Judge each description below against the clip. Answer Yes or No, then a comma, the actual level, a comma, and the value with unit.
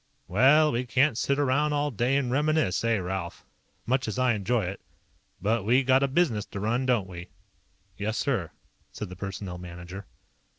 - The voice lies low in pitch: Yes, low, 115 Hz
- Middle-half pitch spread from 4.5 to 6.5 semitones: Yes, wide, 5.6 semitones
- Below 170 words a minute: No, average, 175 wpm